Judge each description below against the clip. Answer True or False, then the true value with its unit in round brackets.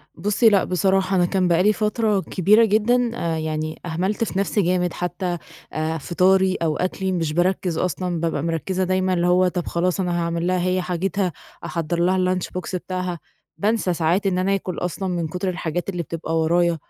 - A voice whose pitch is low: False (180 Hz)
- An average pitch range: False (2.0 semitones)